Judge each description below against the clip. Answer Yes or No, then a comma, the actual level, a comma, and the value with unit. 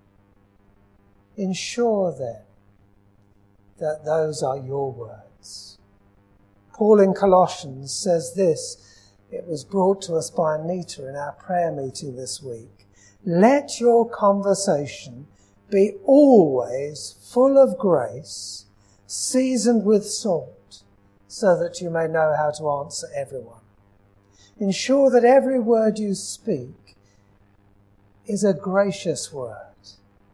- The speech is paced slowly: Yes, slow, 110 wpm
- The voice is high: No, medium, 140 Hz